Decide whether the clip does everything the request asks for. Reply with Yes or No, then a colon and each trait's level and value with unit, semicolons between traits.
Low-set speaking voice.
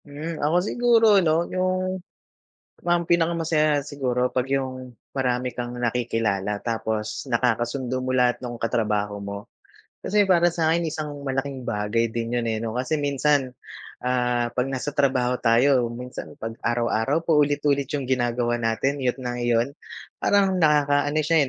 Yes: low, 130 Hz